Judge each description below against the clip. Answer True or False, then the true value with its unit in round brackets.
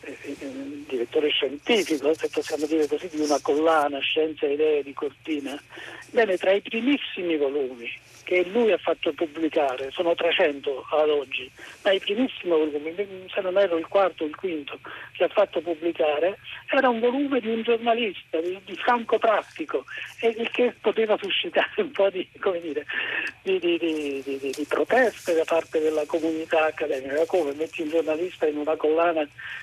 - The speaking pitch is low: False (175 Hz)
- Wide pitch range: True (6.7 semitones)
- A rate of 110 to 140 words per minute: False (160 wpm)